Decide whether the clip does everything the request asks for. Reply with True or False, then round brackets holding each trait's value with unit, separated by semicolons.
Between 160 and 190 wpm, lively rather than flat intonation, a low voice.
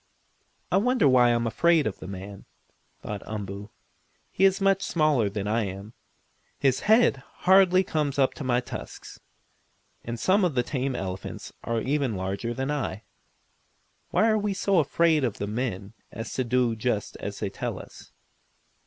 True (170 wpm; 7.7 semitones; 125 Hz)